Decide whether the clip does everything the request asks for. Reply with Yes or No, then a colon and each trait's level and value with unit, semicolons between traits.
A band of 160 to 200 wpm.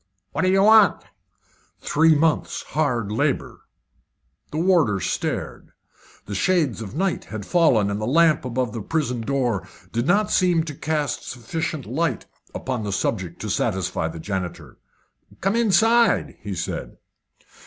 No: average, 145 wpm